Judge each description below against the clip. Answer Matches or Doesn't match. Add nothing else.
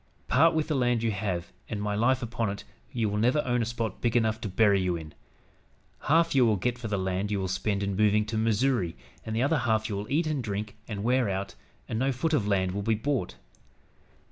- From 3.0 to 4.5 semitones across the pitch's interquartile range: Matches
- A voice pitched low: Matches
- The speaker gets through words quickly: Matches